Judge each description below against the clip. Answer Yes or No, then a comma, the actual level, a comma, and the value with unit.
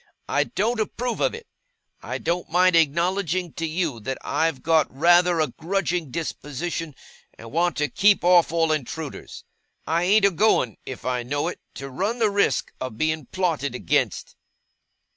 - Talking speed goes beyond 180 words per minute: No, average, 160 wpm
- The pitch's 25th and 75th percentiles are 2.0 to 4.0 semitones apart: Yes, average, 3.7 semitones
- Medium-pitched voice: Yes, medium, 165 Hz